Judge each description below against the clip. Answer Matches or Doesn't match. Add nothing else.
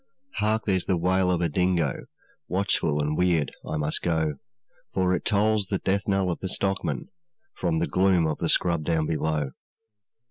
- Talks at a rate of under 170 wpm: Doesn't match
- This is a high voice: Doesn't match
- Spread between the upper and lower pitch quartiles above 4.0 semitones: Doesn't match